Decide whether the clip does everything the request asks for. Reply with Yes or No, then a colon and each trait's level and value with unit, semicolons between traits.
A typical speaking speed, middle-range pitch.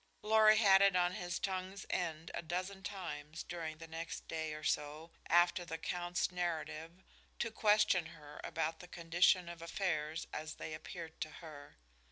Yes: average, 165 wpm; medium, 170 Hz